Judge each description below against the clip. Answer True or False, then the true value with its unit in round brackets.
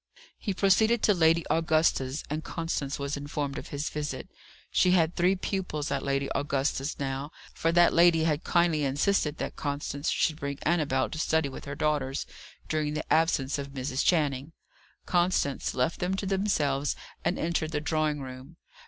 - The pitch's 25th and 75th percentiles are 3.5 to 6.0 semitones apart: False (3.1 semitones)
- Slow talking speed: False (165 wpm)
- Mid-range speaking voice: True (150 Hz)